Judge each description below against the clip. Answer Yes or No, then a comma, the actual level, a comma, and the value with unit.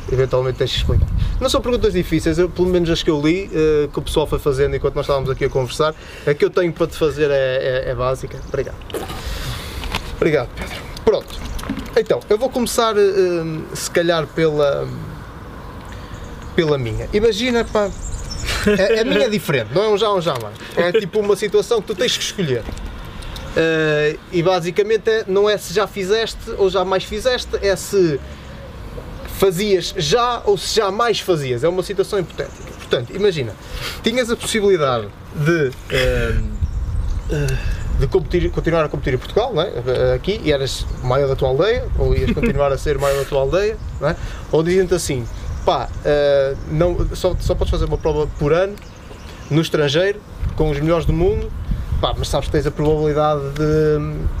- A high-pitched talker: No, medium, 155 Hz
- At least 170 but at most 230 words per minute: Yes, average, 180 wpm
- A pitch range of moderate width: No, wide, 6.6 semitones